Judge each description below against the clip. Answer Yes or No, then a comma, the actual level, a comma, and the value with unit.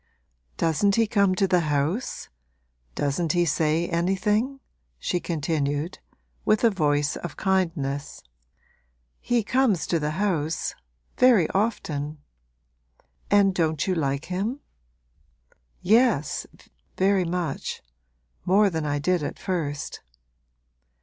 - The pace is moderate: No, slow, 110 wpm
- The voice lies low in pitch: No, medium, 175 Hz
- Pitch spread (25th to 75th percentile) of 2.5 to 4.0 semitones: No, average, 4.8 semitones